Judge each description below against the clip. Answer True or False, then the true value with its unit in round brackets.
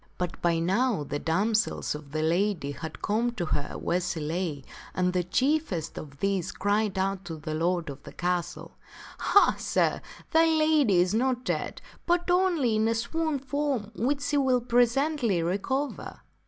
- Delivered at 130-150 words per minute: False (175 wpm)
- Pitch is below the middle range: False (205 Hz)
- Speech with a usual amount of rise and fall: False (7.5 semitones)